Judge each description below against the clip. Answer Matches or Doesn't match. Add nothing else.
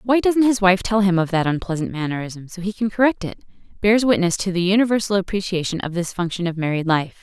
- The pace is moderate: Doesn't match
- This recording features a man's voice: Doesn't match